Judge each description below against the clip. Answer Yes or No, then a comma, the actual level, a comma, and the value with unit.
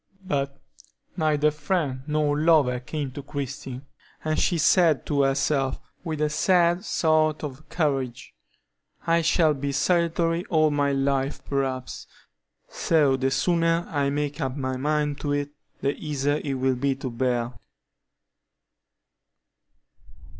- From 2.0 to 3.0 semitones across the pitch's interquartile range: Yes, narrow, 2.5 semitones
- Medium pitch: Yes, medium, 145 Hz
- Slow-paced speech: Yes, slow, 130 wpm